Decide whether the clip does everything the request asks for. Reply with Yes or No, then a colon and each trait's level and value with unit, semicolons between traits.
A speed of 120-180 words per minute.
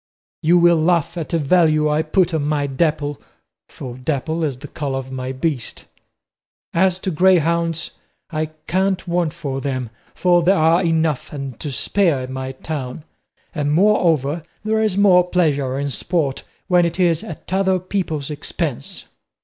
Yes: average, 160 wpm